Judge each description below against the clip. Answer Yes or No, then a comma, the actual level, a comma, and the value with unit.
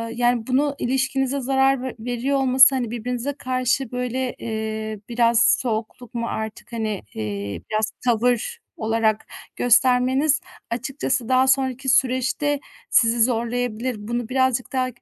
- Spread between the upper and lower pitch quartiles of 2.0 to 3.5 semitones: Yes, narrow, 2.4 semitones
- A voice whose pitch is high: Yes, high, 245 Hz